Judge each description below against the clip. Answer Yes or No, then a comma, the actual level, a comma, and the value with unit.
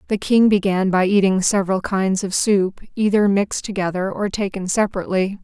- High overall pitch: Yes, high, 195 Hz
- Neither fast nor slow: Yes, average, 165 wpm